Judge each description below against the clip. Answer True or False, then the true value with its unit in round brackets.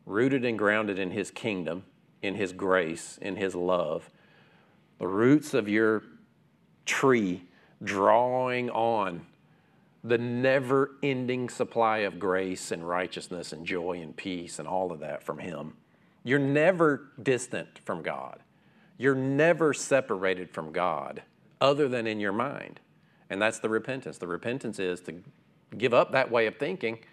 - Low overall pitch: True (115 Hz)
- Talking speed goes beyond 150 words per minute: False (145 wpm)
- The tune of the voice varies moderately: False (6.1 semitones)